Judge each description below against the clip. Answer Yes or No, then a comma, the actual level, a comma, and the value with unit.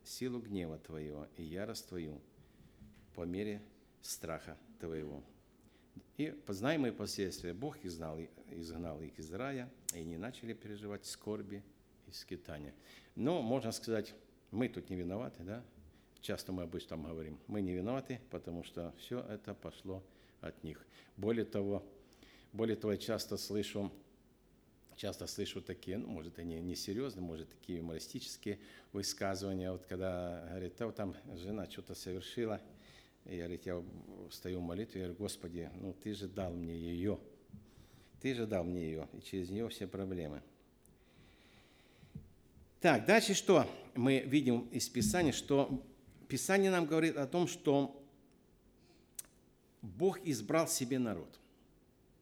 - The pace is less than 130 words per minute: No, average, 135 wpm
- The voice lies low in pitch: Yes, low, 100 Hz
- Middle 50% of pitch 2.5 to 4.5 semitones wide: No, average, 4.9 semitones